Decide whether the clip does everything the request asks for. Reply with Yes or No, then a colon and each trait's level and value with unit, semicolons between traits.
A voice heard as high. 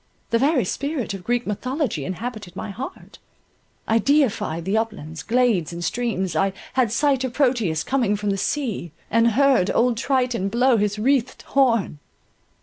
Yes: high, 230 Hz